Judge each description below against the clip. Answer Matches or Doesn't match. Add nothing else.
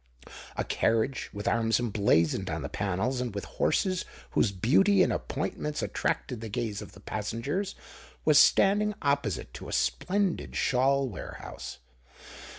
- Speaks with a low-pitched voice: Matches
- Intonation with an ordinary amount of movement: Doesn't match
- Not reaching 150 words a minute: Matches